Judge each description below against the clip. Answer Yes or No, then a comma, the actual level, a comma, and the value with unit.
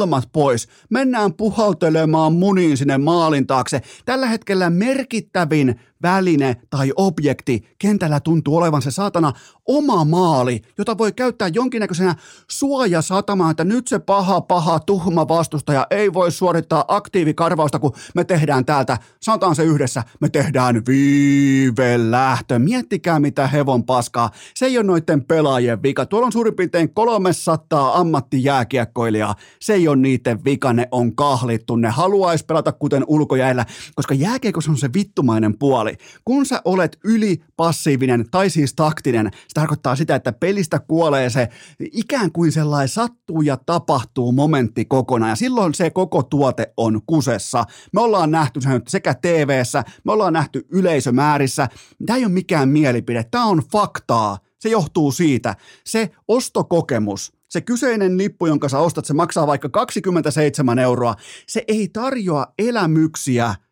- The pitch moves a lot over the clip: Yes, wide, 5.9 semitones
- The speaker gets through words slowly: No, average, 140 wpm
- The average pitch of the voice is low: No, medium, 155 Hz